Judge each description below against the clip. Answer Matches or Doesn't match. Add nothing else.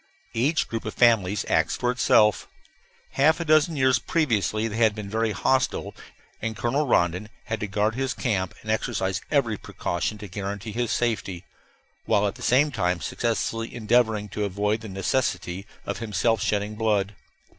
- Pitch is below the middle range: Matches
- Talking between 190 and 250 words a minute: Doesn't match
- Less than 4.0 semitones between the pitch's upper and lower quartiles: Matches